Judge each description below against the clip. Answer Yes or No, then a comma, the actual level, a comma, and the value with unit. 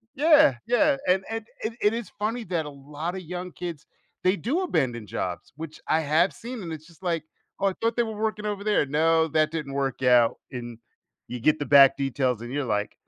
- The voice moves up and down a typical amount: No, wide, 7.1 semitones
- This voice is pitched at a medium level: Yes, medium, 160 Hz